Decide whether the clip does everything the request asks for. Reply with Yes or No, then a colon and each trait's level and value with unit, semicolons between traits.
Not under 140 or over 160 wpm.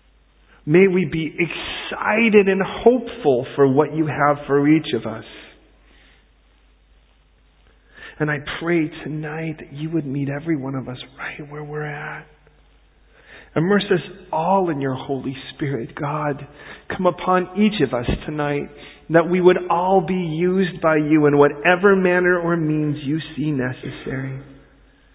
Yes: average, 145 wpm